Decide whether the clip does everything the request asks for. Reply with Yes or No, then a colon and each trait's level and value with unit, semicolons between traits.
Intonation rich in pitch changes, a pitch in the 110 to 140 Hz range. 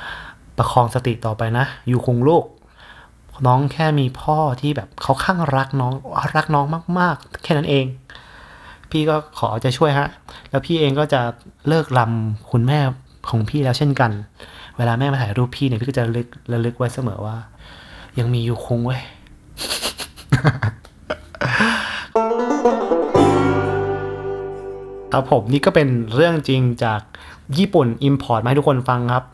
No: average, 3.9 semitones; low, 130 Hz